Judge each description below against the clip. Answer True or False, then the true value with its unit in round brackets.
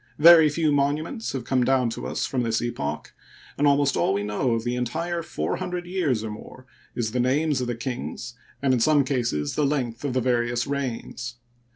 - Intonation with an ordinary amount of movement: True (3.6 semitones)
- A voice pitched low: True (130 Hz)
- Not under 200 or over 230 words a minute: True (205 wpm)